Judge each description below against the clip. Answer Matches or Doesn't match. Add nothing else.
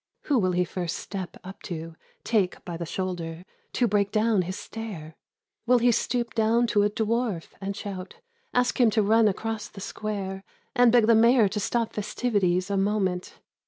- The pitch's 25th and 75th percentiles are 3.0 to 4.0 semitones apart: Matches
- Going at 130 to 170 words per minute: Doesn't match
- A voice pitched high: Matches